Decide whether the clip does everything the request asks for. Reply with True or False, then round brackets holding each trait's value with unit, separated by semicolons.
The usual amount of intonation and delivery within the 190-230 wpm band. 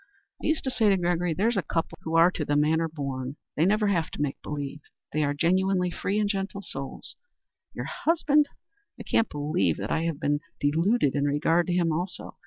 True (4.9 semitones; 205 wpm)